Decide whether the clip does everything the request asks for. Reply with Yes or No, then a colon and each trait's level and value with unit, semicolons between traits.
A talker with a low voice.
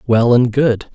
Yes: low, 120 Hz